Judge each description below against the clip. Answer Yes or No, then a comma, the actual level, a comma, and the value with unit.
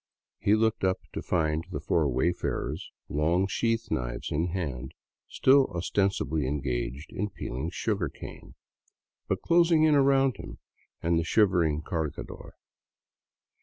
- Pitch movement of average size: No, wide, 6.6 semitones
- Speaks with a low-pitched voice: Yes, very low, 85 Hz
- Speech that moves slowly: Yes, slow, 125 wpm